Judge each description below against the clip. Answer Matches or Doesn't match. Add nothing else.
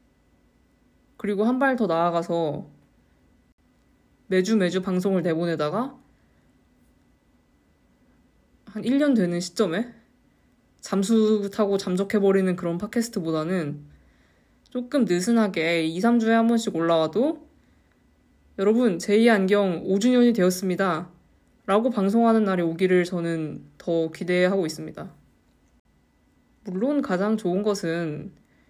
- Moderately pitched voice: Doesn't match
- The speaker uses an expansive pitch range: Doesn't match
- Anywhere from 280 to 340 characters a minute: Doesn't match